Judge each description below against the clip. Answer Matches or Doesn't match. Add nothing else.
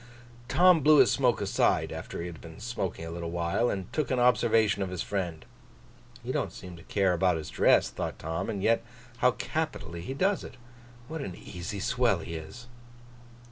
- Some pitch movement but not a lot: Doesn't match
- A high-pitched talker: Doesn't match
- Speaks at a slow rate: Doesn't match